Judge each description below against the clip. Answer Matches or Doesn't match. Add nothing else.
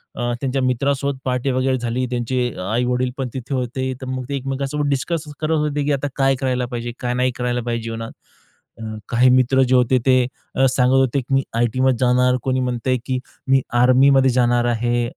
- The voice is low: Matches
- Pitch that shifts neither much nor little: Doesn't match